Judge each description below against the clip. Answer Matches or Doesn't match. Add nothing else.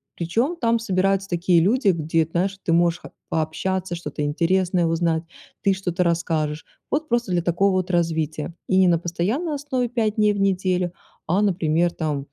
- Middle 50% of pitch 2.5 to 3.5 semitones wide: Matches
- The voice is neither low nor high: Matches